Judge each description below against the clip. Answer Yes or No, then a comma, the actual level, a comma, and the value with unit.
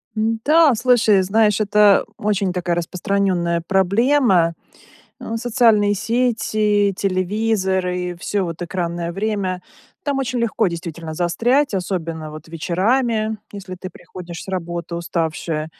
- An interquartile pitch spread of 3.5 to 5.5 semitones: Yes, average, 4.2 semitones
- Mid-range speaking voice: No, high, 195 Hz